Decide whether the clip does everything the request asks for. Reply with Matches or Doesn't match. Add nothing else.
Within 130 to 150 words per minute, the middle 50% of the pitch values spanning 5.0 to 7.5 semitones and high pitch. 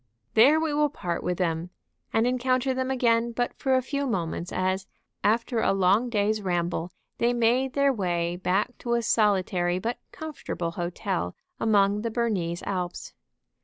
Doesn't match